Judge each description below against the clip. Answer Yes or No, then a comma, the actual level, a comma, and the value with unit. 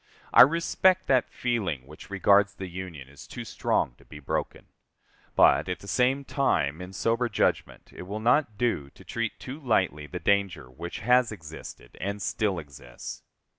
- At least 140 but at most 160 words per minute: No, average, 170 wpm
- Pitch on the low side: Yes, low, 100 Hz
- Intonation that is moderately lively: No, wide, 7.6 semitones